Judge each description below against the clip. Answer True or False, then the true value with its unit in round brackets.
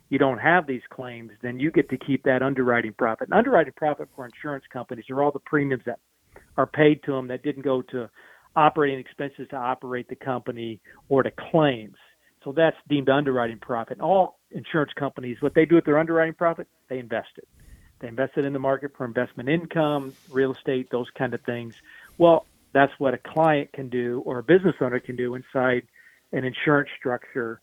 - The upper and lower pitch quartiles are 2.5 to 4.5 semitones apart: True (2.8 semitones)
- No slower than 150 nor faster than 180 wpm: False (200 wpm)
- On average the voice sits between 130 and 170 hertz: True (135 Hz)